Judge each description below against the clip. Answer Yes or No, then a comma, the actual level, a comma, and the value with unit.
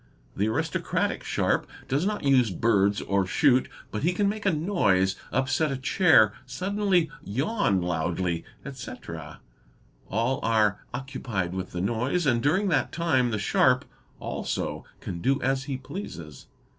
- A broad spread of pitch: Yes, wide, 7.4 semitones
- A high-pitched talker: No, low, 125 Hz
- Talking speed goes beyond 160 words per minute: No, average, 140 wpm